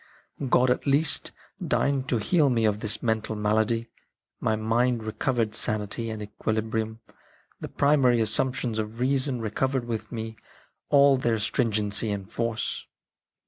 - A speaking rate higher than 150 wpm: No, average, 145 wpm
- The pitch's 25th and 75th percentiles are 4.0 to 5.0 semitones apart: No, average, 2.7 semitones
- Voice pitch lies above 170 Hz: No, low, 115 Hz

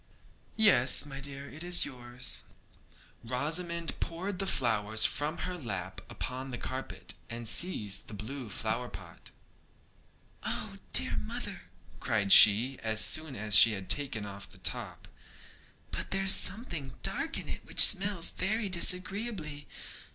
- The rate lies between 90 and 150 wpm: Yes, slow, 135 wpm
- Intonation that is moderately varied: No, wide, 7.8 semitones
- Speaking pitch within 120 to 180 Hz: Yes, low, 135 Hz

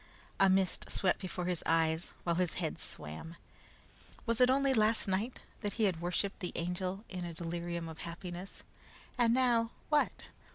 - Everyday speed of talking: Yes, average, 165 wpm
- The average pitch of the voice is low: No, medium, 185 Hz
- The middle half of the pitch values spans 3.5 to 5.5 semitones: Yes, average, 4.2 semitones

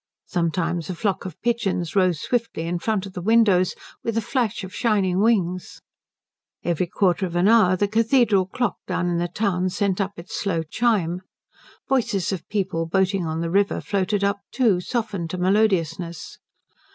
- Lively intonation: No, average, 3.4 semitones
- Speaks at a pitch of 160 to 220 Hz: Yes, high, 190 Hz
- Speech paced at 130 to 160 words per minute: No, average, 170 wpm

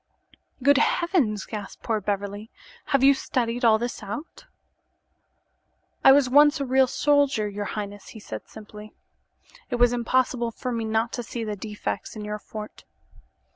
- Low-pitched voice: No, high, 230 Hz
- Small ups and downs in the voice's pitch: No, average, 3.7 semitones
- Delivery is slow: No, average, 155 wpm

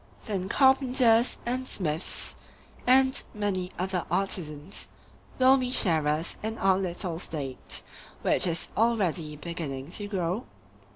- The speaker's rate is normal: No, slow, 115 wpm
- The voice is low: No, high, 190 Hz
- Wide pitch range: Yes, wide, 6.1 semitones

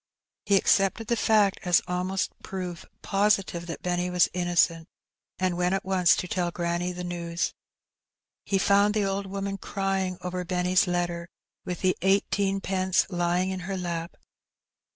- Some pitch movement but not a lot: No, narrow, 1.8 semitones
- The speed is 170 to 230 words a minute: No, average, 150 wpm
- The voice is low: No, medium, 185 Hz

